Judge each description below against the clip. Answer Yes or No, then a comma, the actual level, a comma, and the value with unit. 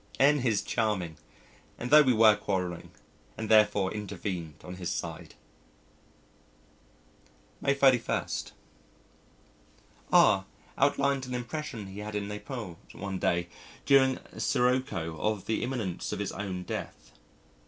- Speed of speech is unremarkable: No, slow, 120 wpm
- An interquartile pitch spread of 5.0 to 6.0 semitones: Yes, average, 5.3 semitones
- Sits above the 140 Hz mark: No, low, 105 Hz